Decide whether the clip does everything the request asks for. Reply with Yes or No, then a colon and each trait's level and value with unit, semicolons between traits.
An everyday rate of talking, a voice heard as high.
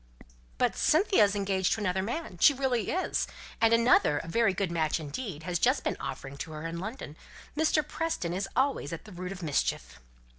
Yes: average, 195 wpm; high, 195 Hz